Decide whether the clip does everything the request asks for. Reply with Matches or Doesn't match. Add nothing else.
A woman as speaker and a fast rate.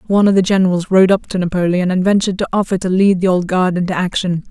Matches